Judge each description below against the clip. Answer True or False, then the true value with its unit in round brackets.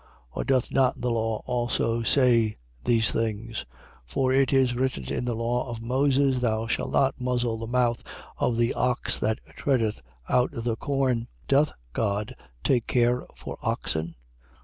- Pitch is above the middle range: False (120 Hz)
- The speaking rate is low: False (160 wpm)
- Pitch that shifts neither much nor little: False (2.1 semitones)